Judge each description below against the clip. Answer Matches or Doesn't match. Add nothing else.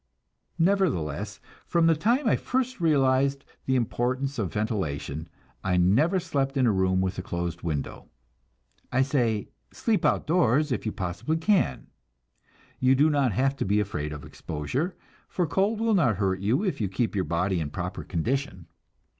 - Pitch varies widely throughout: Matches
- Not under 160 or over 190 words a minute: Matches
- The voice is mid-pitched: Doesn't match